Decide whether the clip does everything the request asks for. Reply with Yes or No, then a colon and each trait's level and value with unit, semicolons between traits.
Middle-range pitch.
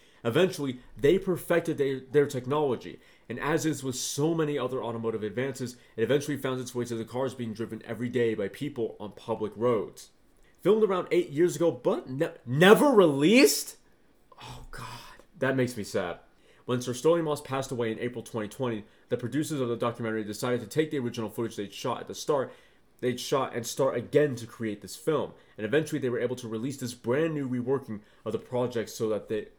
No: low, 125 Hz